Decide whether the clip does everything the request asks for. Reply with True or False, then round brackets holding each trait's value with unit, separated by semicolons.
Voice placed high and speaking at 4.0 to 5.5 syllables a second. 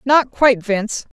True (240 Hz; 5.0 syllables/s)